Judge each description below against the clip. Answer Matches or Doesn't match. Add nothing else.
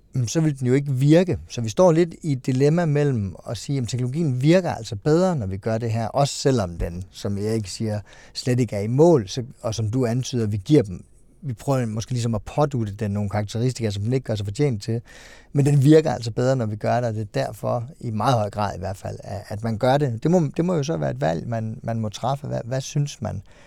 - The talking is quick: Matches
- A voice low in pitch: Matches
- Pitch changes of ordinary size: Matches